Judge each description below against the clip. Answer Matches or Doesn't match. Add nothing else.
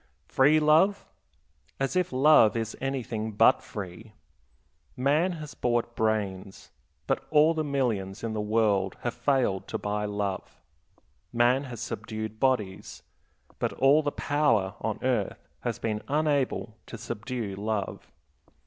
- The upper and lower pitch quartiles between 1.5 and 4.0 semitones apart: Doesn't match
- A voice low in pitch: Matches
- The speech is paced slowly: Matches